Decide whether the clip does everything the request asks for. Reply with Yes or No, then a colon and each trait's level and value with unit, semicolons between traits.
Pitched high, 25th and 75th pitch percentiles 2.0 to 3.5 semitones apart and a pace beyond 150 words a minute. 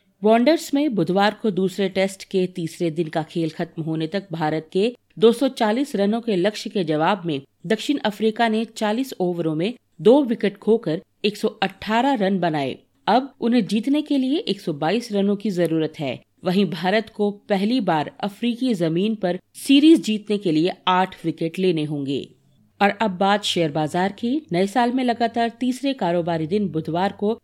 No: high, 200 Hz; average, 4.8 semitones; average, 165 wpm